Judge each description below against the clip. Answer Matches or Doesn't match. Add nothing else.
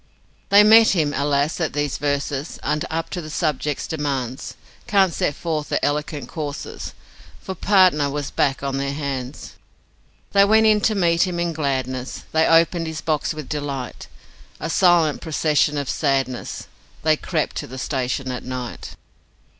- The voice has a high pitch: Doesn't match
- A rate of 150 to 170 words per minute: Matches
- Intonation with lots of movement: Doesn't match